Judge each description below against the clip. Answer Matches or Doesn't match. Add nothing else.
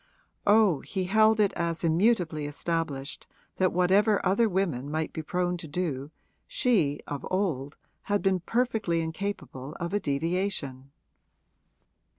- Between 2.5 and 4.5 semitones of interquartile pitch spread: Doesn't match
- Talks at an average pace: Doesn't match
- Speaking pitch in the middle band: Matches